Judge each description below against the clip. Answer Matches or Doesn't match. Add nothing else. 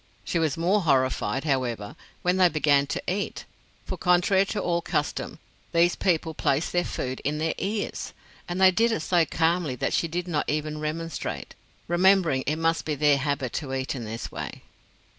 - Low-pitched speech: Doesn't match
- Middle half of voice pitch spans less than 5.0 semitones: Matches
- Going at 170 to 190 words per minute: Matches